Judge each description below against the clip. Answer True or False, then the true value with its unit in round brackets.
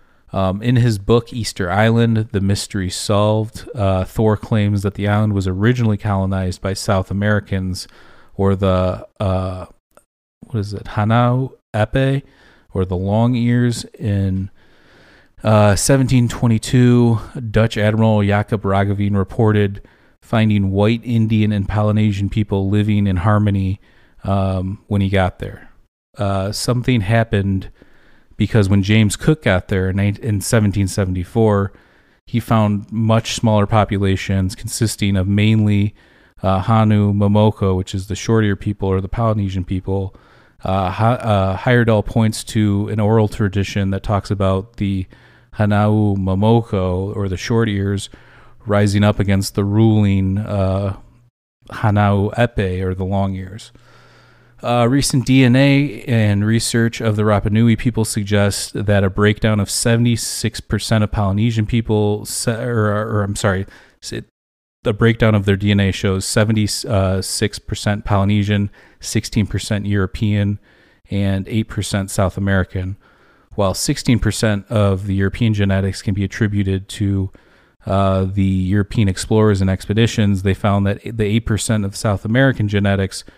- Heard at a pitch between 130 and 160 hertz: False (105 Hz)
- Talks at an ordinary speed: False (130 wpm)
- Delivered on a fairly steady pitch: True (2.3 semitones)